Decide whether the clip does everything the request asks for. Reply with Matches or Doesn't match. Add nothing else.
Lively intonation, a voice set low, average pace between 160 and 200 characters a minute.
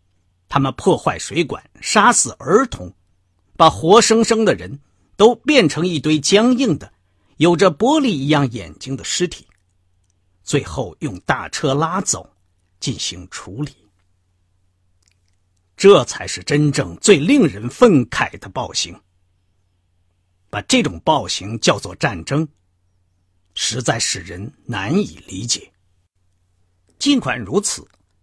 Matches